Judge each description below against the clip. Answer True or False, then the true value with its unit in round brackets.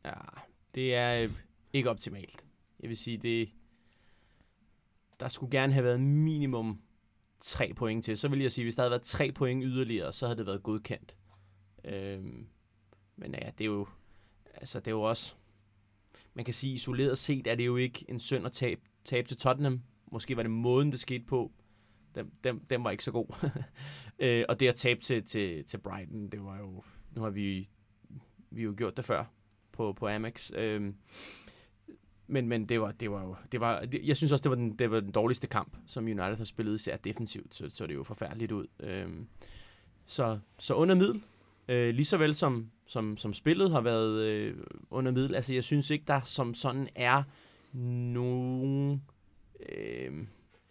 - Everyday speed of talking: True (190 wpm)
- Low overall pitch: True (115 Hz)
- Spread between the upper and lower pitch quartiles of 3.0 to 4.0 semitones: True (3.7 semitones)